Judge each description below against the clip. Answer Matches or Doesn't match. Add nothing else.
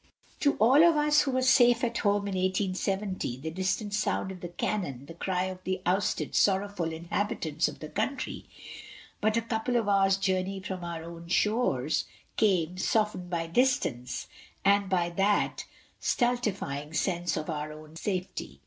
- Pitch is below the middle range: Doesn't match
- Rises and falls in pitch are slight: Doesn't match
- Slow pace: Doesn't match